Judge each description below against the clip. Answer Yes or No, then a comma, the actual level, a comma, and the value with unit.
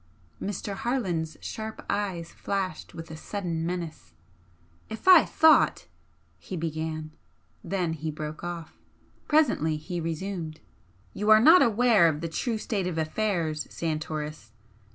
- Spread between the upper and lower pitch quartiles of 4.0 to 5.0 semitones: Yes, average, 4.7 semitones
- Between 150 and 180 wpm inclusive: No, slow, 135 wpm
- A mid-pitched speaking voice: Yes, medium, 170 Hz